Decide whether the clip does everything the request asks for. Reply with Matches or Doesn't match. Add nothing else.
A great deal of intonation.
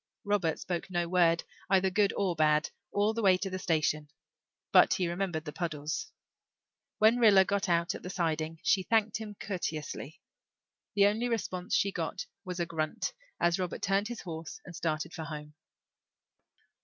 Doesn't match